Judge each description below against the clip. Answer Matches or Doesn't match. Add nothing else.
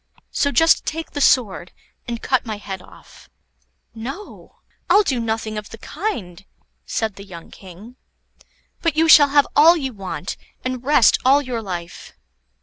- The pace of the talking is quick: Doesn't match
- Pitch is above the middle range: Matches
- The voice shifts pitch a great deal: Matches